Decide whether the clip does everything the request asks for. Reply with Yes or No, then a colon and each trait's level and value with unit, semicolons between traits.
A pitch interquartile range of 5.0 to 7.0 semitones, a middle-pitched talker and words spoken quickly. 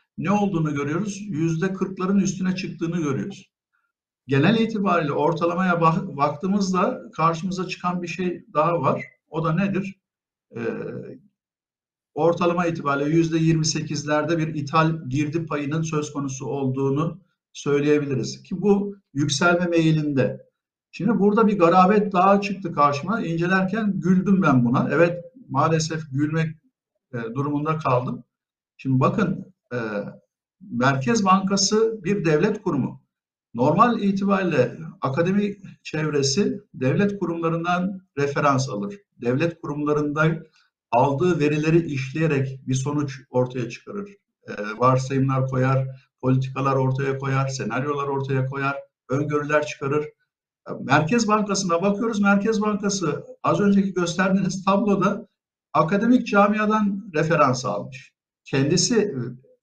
No: wide, 5.5 semitones; medium, 165 Hz; average, 105 wpm